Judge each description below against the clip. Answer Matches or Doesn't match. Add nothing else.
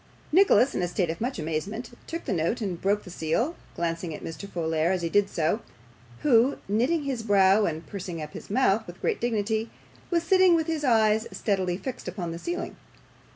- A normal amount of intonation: Doesn't match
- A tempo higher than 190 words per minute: Matches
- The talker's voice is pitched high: Matches